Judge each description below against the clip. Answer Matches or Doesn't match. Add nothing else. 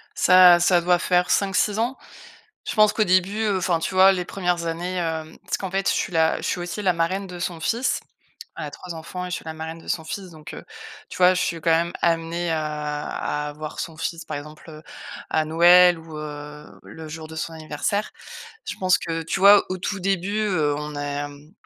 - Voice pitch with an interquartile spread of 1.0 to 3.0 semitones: Matches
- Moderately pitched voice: Matches